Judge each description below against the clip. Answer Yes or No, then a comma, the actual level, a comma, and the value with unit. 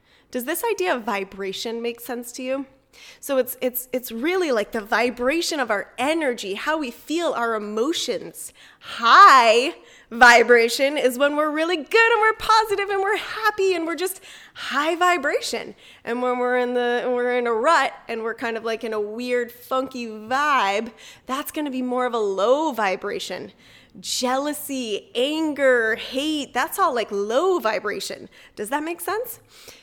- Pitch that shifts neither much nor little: No, wide, 6.0 semitones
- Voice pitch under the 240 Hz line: No, very high, 260 Hz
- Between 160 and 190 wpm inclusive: Yes, average, 165 wpm